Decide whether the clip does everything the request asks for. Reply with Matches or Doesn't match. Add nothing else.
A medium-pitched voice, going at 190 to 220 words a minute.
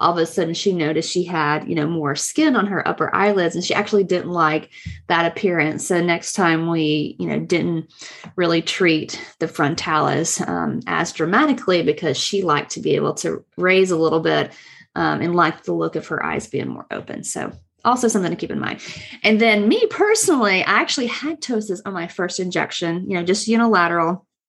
Matches